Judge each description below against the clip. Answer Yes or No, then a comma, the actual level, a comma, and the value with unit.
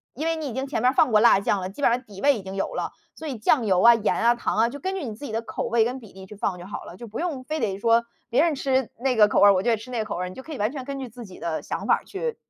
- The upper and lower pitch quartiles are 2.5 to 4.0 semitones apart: No, average, 4.6 semitones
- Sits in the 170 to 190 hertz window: No, high, 235 Hz